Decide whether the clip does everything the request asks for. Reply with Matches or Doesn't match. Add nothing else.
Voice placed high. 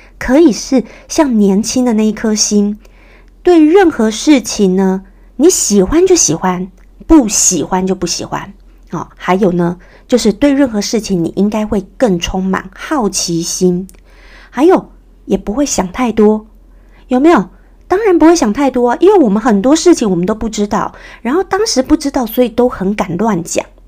Matches